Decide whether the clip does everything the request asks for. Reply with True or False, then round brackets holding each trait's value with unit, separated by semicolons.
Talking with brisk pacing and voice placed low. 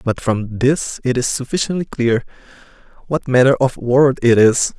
False (165 wpm; 125 Hz)